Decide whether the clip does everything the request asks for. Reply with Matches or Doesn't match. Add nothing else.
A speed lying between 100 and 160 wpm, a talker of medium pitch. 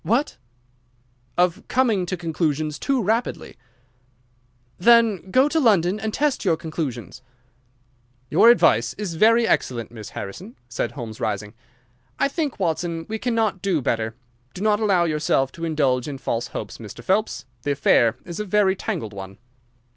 Matches